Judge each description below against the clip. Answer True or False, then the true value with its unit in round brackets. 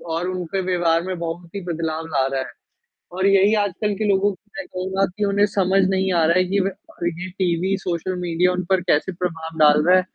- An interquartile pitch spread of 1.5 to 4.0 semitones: True (2.4 semitones)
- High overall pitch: False (180 Hz)